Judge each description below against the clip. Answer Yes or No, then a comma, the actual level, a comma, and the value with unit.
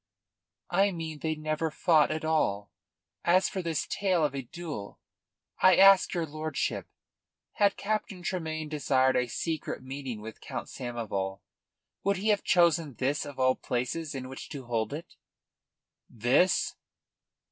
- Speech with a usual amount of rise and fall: Yes, average, 5.0 semitones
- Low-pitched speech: No, medium, 155 Hz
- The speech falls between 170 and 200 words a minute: No, average, 145 wpm